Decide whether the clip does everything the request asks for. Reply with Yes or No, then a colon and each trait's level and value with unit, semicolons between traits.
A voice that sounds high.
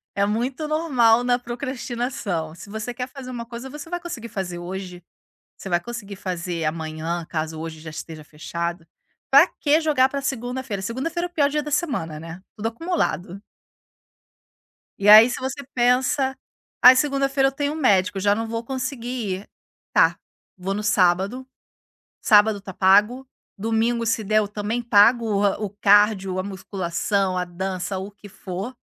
Yes: high, 215 Hz